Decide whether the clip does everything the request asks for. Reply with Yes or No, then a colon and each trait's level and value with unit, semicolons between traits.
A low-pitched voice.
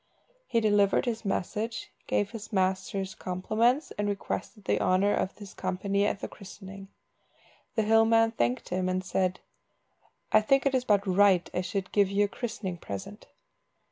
No: high, 200 Hz